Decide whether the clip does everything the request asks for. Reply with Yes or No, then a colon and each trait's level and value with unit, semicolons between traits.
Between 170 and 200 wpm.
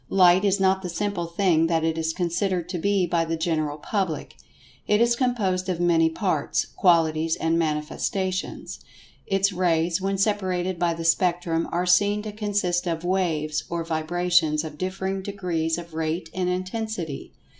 No: average, 160 wpm